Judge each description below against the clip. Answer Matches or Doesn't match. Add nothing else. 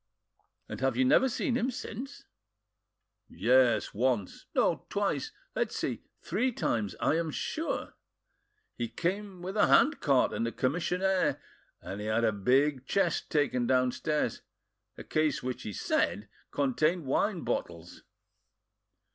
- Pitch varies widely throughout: Matches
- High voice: Doesn't match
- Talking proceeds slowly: Matches